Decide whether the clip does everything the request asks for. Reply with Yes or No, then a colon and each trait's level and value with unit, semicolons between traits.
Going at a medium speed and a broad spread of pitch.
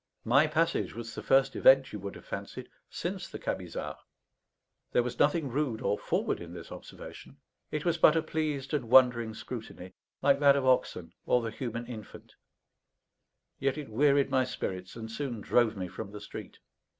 No: average, 175 wpm; average, 4.0 semitones